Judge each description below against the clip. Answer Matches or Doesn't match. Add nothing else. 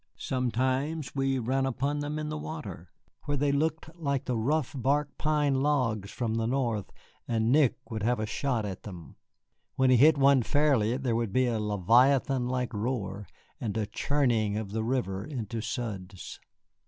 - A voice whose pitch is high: Doesn't match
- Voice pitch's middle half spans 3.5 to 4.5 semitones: Matches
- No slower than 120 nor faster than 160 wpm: Doesn't match